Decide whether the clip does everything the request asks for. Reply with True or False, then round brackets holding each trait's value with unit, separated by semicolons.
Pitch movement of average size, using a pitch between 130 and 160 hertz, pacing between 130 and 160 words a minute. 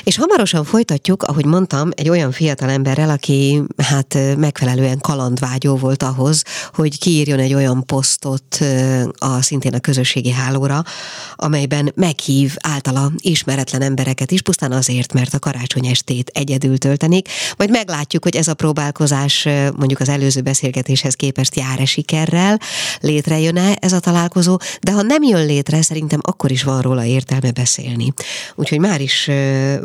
True (3.1 semitones; 140 Hz; 145 wpm)